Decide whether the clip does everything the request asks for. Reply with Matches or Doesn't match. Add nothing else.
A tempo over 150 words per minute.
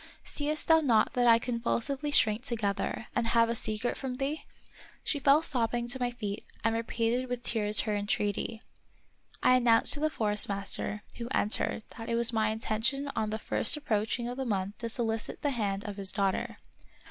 Matches